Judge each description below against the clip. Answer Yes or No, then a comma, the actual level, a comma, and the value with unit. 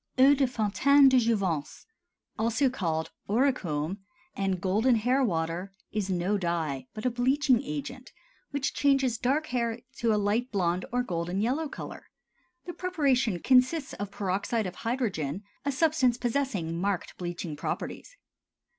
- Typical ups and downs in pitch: No, wide, 6.2 semitones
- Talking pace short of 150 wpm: Yes, average, 140 wpm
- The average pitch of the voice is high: Yes, high, 225 Hz